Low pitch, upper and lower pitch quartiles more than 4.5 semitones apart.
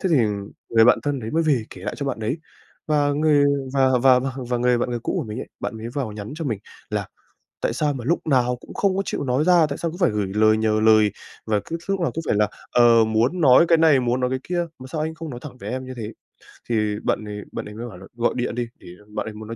Yes: low, 125 Hz; average, 5.1 semitones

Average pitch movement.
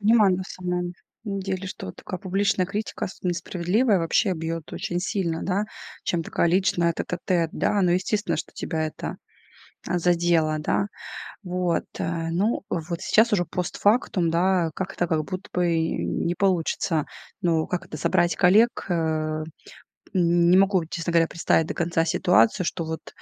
No: narrow, 2.3 semitones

